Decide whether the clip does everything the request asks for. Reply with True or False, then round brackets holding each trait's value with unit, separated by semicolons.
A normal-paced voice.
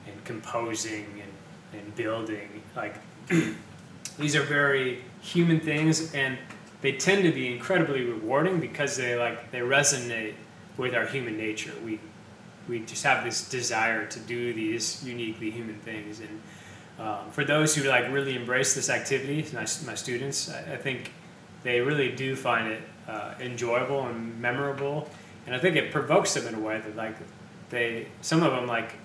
True (165 wpm)